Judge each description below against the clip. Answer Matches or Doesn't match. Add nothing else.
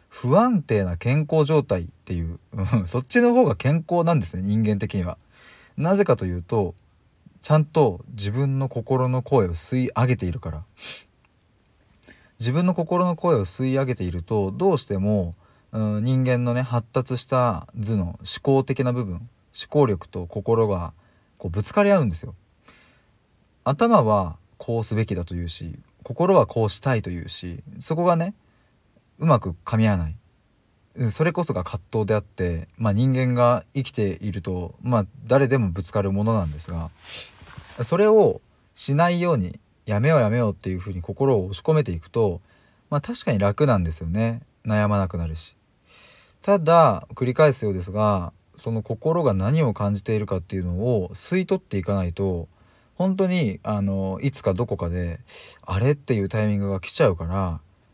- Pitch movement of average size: Doesn't match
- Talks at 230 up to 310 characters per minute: Doesn't match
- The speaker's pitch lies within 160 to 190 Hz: Doesn't match